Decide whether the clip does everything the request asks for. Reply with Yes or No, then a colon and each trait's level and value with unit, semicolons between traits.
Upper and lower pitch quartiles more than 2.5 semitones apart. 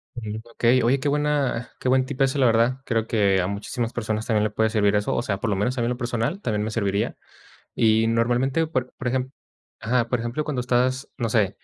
Yes: average, 2.9 semitones